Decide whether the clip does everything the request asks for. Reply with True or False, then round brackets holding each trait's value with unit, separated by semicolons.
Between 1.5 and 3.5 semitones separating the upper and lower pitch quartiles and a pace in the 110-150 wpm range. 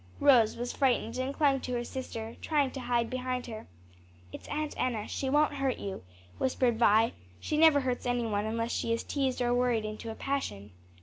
False (2.9 semitones; 195 wpm)